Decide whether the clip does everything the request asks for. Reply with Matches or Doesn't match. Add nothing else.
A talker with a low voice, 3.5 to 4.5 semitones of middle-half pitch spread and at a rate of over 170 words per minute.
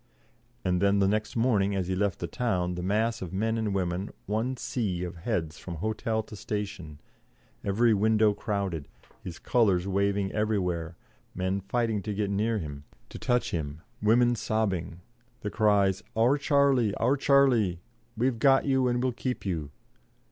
Doesn't match